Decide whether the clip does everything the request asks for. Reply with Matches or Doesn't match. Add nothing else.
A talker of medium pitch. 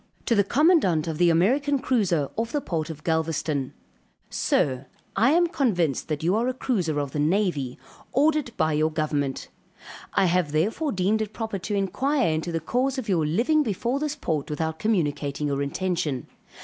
Matches